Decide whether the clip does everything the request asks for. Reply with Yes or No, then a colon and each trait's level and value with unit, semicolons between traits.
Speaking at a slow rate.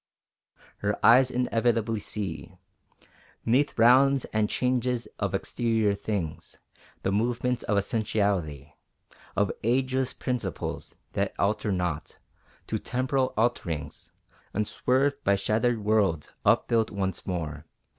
Yes: slow, 105 wpm